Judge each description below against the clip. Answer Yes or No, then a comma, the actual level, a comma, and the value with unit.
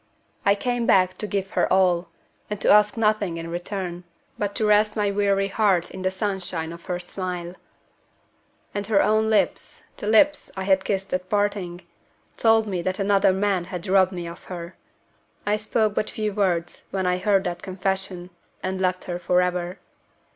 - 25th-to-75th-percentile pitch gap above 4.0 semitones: No, narrow, 2.4 semitones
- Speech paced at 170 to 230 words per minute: Yes, average, 175 wpm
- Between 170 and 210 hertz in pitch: Yes, high, 190 Hz